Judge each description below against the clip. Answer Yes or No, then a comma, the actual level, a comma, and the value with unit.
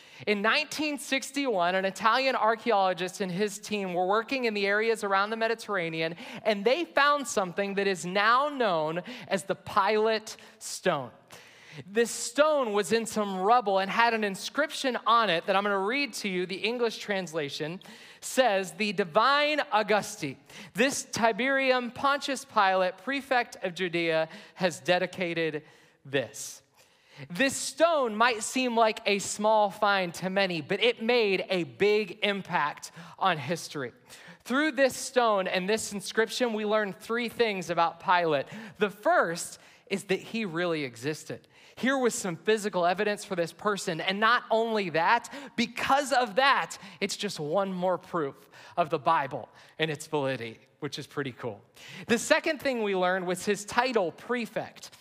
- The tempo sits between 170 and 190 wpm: No, average, 155 wpm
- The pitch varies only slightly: No, average, 4.7 semitones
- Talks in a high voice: Yes, high, 205 Hz